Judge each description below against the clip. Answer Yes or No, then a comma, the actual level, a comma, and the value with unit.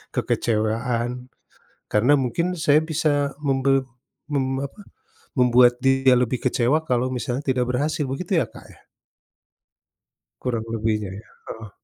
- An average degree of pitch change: Yes, average, 3.2 semitones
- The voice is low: Yes, low, 130 Hz